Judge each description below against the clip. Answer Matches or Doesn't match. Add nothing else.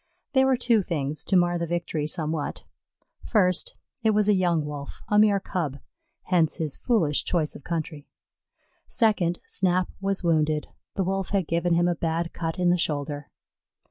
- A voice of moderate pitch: Matches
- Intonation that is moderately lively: Matches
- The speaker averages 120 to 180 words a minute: Matches